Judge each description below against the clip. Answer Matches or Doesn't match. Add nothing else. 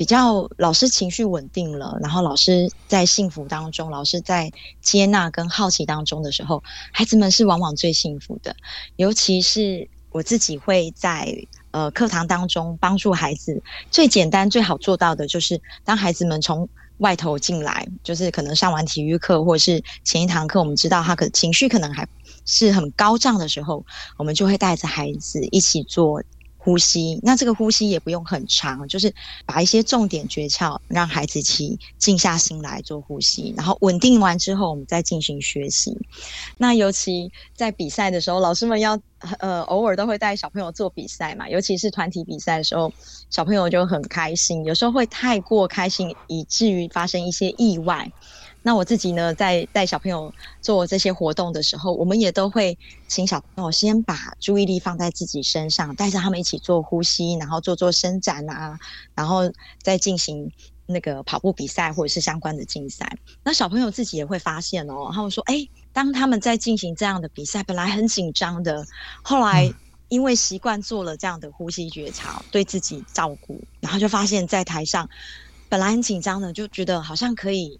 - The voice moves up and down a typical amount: Matches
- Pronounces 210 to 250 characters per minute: Doesn't match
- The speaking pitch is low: Doesn't match